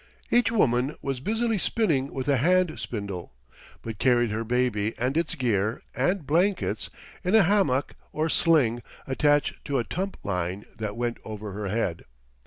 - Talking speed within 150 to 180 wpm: Yes, average, 160 wpm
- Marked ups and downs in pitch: Yes, wide, 7.2 semitones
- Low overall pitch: Yes, low, 130 Hz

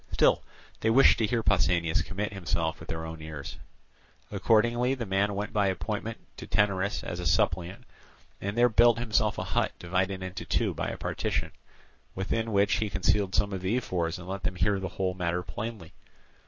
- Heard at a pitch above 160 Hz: No, low, 100 Hz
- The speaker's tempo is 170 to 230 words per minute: Yes, average, 185 wpm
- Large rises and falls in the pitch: No, average, 3.3 semitones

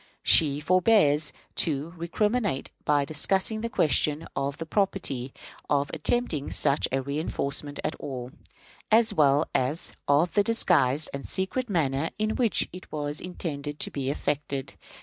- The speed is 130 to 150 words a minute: Yes, average, 140 wpm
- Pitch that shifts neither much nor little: Yes, average, 5.0 semitones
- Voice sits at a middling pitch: Yes, medium, 150 Hz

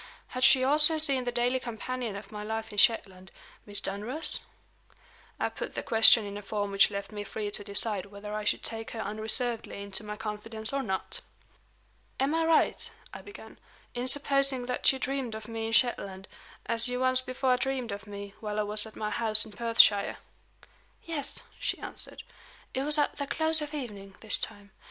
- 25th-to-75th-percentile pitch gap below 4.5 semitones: Yes, average, 3.8 semitones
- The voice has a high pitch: Yes, high, 225 Hz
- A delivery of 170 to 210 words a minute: Yes, average, 190 wpm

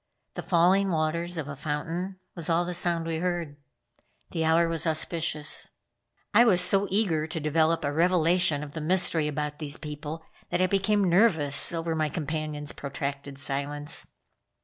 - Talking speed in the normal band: Yes, average, 160 wpm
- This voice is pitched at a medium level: Yes, medium, 160 Hz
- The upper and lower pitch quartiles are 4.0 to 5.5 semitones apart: No, average, 2.9 semitones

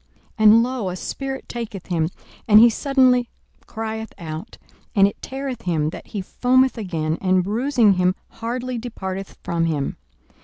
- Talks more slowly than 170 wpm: Yes, average, 155 wpm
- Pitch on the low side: No, high, 220 Hz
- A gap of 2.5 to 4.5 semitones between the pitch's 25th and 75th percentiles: No, average, 5.3 semitones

